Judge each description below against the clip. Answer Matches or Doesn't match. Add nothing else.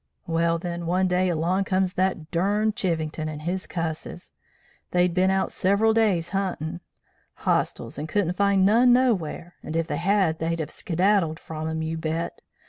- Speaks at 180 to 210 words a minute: Doesn't match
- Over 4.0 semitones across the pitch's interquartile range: Doesn't match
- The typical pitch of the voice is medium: Matches